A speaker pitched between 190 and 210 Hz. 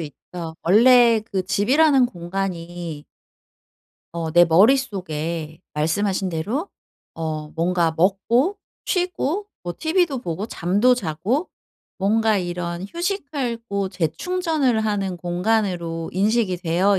Yes: high, 195 Hz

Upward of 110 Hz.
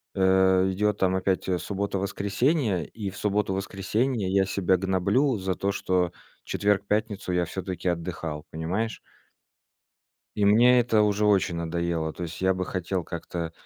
No: very low, 95 Hz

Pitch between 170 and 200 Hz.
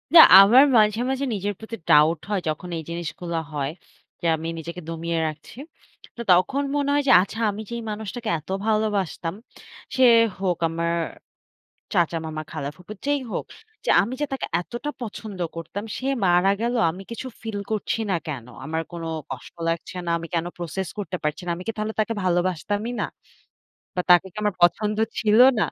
Yes: high, 190 Hz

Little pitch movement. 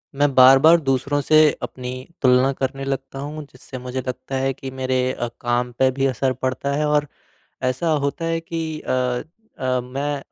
Yes: narrow, 2.1 semitones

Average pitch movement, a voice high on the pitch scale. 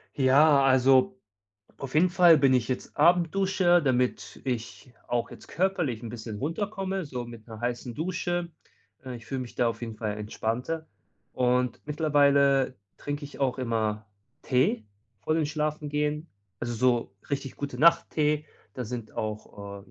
No: average, 4.6 semitones; low, 135 Hz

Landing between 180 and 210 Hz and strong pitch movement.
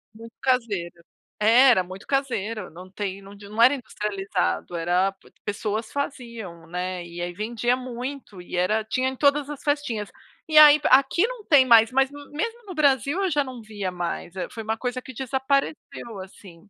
No: high, 230 Hz; wide, 5.8 semitones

